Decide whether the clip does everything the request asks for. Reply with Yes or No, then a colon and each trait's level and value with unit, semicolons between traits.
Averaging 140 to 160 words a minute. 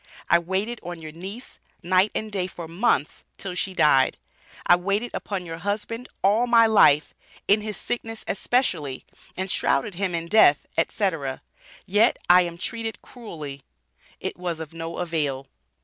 Yes: average, 155 wpm